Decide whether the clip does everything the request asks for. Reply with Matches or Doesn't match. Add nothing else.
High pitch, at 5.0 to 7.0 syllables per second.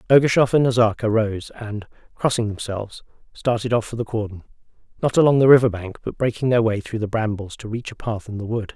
Doesn't match